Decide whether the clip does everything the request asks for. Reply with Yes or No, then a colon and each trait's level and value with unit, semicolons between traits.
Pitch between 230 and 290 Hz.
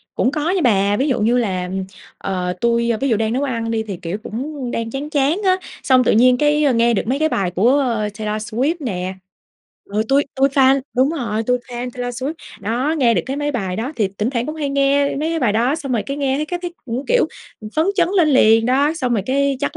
Yes: very high, 255 Hz